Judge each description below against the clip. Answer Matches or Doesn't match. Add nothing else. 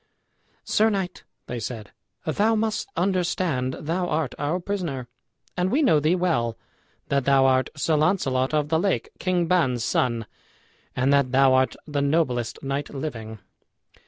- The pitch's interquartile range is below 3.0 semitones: Doesn't match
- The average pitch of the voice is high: Doesn't match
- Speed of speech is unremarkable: Matches